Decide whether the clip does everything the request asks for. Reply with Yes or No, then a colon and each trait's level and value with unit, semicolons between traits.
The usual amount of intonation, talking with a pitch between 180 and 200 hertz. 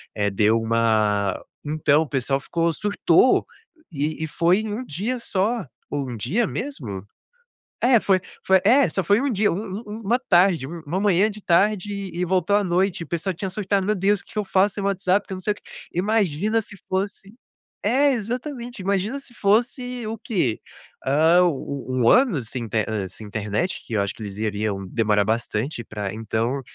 No: wide, 8.7 semitones; medium, 185 Hz